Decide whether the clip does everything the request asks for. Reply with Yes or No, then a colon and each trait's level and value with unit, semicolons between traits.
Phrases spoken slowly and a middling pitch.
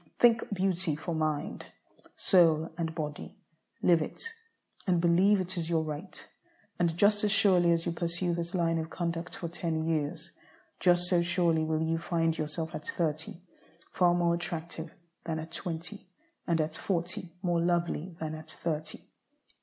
No: average, 160 wpm; medium, 170 Hz